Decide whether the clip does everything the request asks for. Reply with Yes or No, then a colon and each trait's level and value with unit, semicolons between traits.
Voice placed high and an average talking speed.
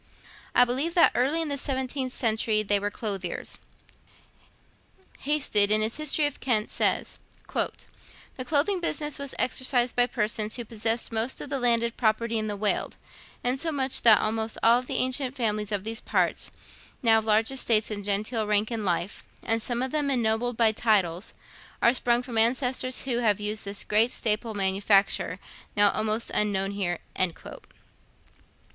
Yes: high, 230 Hz; average, 160 wpm